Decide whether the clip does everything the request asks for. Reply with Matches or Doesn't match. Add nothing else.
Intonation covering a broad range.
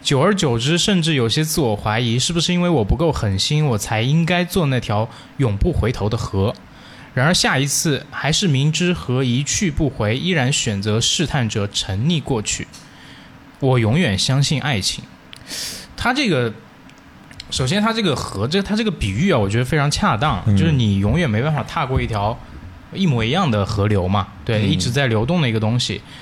Matches